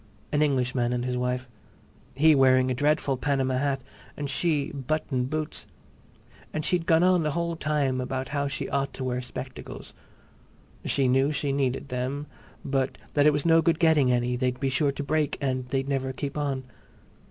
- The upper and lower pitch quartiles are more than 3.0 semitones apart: No, narrow, 2.6 semitones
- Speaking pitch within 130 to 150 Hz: Yes, medium, 140 Hz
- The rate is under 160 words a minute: No, average, 180 wpm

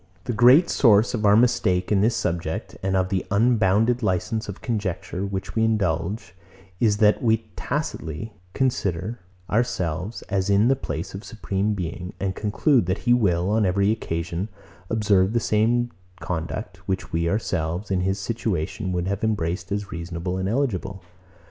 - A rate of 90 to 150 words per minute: No, average, 160 wpm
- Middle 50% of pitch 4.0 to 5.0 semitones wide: No, average, 3.5 semitones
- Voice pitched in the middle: No, low, 100 Hz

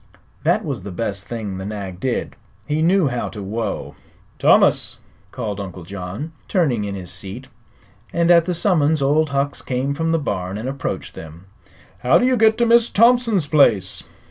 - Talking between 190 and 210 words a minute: No, average, 175 wpm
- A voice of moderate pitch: No, low, 130 Hz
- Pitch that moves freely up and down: Yes, wide, 8.7 semitones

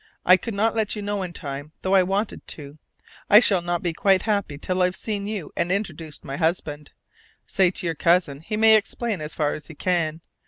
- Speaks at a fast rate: Yes, fast, 220 wpm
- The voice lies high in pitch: No, medium, 180 Hz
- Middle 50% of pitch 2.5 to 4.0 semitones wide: No, average, 4.4 semitones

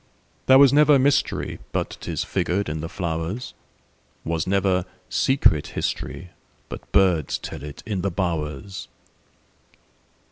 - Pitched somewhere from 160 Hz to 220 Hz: No, very low, 90 Hz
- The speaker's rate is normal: No, slow, 105 wpm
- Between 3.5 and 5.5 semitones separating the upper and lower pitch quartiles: Yes, average, 4.5 semitones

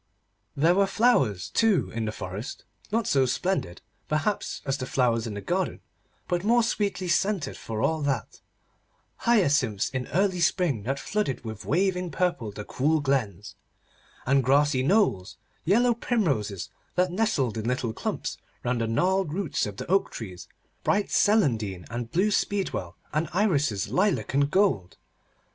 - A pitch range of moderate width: No, wide, 9.0 semitones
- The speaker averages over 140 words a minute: Yes, average, 150 wpm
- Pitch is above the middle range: No, medium, 145 Hz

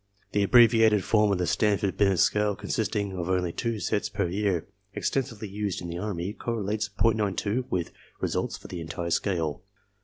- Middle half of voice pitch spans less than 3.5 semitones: Yes, average, 2.7 semitones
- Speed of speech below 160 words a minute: No, average, 165 wpm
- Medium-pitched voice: No, low, 100 Hz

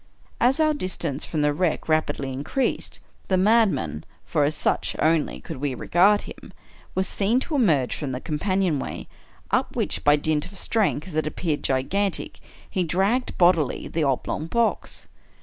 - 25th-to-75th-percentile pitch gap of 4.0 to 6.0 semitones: Yes, average, 5.1 semitones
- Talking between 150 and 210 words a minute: Yes, average, 160 wpm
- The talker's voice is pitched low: No, medium, 165 Hz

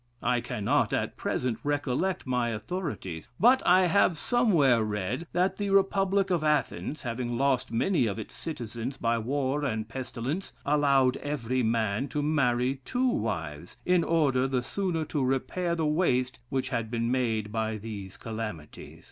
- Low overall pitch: Yes, low, 130 Hz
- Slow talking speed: No, average, 155 wpm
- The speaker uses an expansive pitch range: Yes, wide, 5.7 semitones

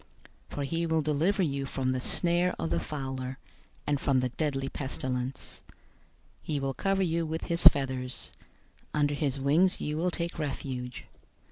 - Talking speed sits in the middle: Yes, average, 165 wpm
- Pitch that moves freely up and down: No, average, 3.8 semitones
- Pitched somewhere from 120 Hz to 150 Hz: Yes, medium, 140 Hz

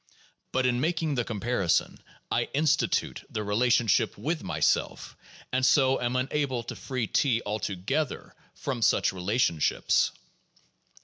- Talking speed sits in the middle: No, slow, 125 wpm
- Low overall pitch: Yes, low, 125 Hz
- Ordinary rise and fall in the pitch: Yes, average, 3.8 semitones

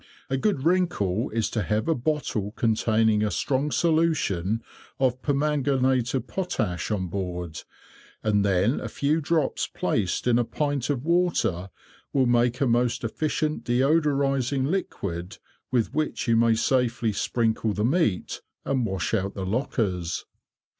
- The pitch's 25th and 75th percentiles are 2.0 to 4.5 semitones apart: No, average, 5.2 semitones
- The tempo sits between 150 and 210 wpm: No, average, 140 wpm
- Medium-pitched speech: No, low, 120 Hz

